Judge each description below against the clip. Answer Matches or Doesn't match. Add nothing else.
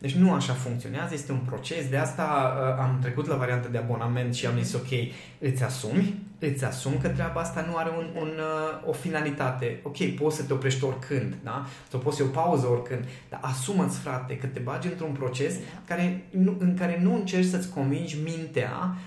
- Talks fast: Matches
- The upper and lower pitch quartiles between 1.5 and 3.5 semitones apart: Doesn't match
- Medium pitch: Matches